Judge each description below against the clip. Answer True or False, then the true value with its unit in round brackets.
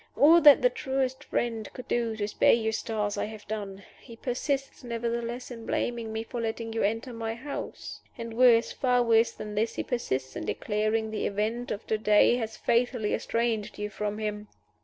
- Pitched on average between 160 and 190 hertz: False (225 Hz)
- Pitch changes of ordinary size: False (2.1 semitones)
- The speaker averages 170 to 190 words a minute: True (185 wpm)